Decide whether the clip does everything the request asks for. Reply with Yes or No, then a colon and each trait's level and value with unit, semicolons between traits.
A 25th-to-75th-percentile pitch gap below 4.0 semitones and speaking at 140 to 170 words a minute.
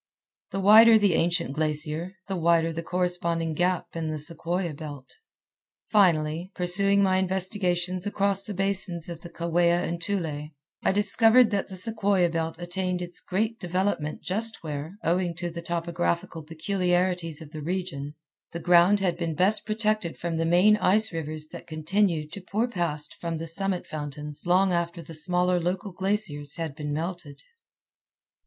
Yes: average, 2.9 semitones; average, 160 wpm